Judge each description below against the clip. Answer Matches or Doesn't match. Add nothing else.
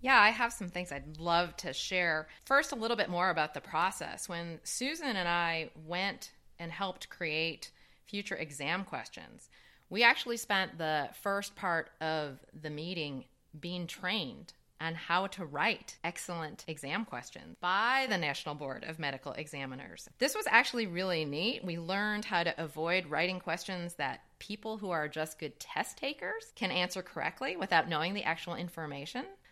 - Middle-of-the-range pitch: Matches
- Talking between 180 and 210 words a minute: Doesn't match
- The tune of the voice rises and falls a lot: Doesn't match